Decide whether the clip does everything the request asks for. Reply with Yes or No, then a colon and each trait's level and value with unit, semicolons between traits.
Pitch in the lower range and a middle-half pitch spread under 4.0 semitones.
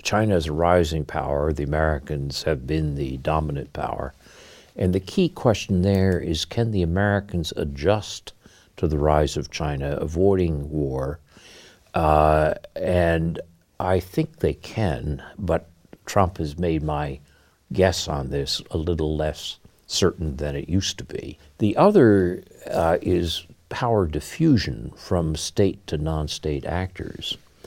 Yes: very low, 80 Hz; average, 3.6 semitones